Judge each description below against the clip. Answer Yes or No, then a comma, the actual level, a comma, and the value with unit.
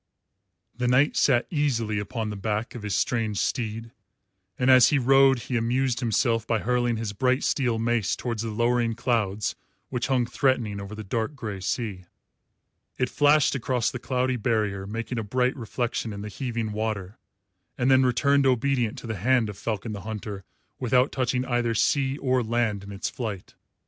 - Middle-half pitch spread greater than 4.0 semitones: No, average, 3.0 semitones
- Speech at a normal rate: Yes, average, 175 wpm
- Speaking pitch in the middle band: No, low, 120 Hz